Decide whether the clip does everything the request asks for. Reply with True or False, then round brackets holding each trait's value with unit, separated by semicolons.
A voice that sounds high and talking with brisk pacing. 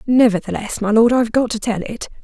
True (225 Hz; 215 wpm)